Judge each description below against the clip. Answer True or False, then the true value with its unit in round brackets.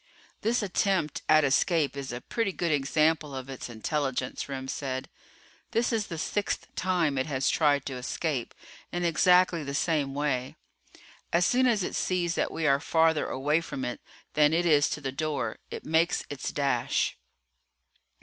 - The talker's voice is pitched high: False (150 Hz)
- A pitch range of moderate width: True (4.0 semitones)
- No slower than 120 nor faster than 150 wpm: False (170 wpm)